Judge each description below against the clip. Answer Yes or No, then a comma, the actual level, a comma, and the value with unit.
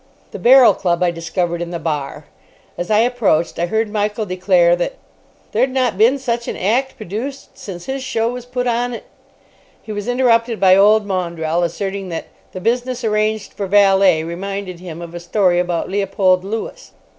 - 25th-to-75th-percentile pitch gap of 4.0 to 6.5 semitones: Yes, average, 4.8 semitones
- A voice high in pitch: Yes, high, 200 Hz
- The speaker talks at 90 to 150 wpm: No, average, 180 wpm